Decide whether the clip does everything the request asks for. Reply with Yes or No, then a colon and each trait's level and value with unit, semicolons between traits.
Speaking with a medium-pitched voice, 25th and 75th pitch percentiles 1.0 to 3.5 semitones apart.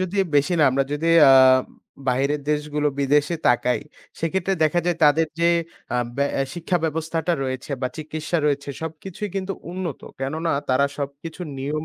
Yes: medium, 155 Hz; average, 3.1 semitones